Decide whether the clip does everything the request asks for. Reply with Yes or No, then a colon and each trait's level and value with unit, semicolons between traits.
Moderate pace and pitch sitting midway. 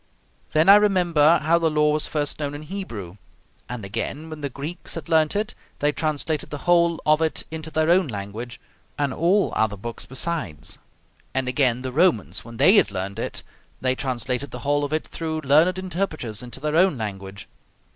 Yes: average, 185 wpm; medium, 150 Hz